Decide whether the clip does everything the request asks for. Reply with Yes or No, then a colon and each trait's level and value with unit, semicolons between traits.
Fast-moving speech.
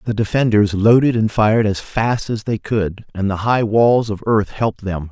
Yes: fast, 210 wpm